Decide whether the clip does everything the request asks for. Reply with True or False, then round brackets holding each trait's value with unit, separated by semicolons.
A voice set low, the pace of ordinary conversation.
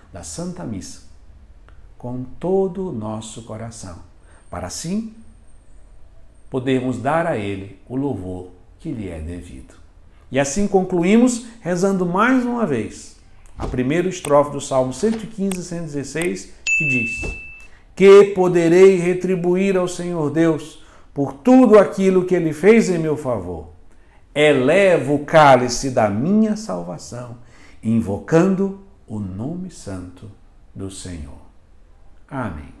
False (130 Hz; 115 wpm)